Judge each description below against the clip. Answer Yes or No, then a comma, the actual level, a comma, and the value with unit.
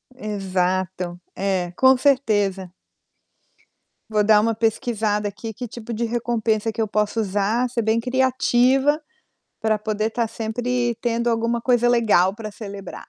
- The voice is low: No, high, 220 Hz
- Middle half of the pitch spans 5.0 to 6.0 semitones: No, average, 2.7 semitones